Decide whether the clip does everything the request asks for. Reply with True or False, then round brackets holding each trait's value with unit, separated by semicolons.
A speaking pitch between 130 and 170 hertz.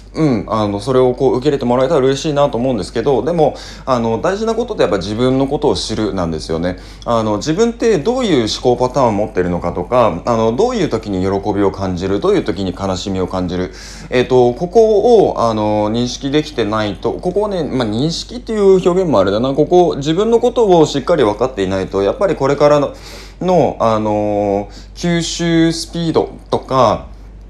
False (120 Hz)